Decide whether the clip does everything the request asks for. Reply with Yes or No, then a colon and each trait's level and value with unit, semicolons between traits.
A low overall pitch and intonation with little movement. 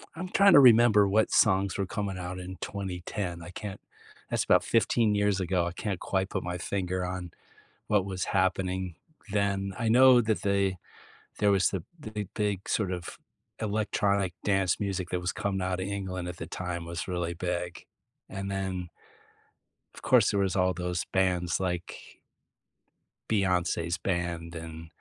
Yes: very low, 95 Hz; narrow, 2.2 semitones